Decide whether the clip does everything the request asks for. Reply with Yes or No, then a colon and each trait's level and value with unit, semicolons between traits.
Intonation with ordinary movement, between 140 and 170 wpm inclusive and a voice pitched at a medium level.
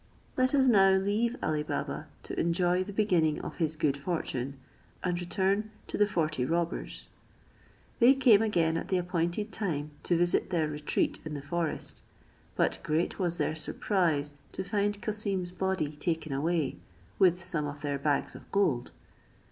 Yes: average, 4.4 semitones; average, 160 wpm; medium, 175 Hz